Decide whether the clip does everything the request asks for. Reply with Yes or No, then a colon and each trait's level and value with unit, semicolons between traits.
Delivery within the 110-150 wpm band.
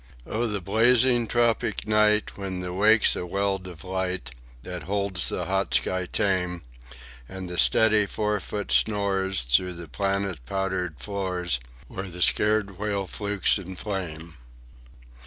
Yes: average, 140 wpm